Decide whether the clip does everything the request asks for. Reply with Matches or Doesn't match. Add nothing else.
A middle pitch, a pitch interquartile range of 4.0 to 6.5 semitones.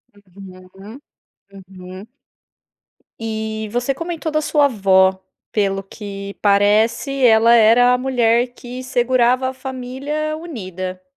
Doesn't match